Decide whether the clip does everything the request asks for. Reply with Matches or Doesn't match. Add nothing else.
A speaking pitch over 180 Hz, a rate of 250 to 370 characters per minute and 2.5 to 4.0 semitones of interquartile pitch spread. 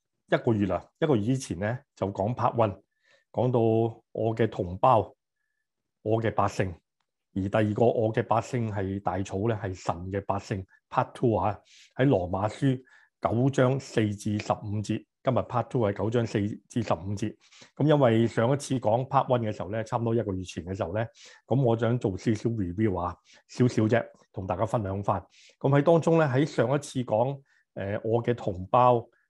Doesn't match